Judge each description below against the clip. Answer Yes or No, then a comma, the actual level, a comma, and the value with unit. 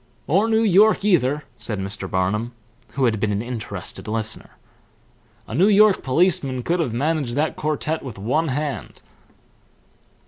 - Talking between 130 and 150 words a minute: Yes, average, 145 wpm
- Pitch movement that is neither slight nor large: No, wide, 7.2 semitones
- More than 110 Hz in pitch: Yes, low, 135 Hz